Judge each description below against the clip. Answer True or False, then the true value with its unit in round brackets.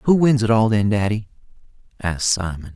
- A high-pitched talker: False (105 Hz)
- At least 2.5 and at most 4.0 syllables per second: False (5.5 syllables/s)